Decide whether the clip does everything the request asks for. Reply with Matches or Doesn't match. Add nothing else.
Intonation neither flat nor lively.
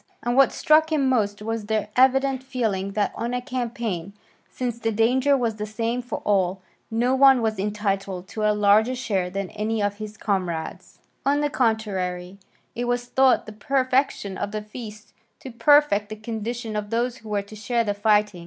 Matches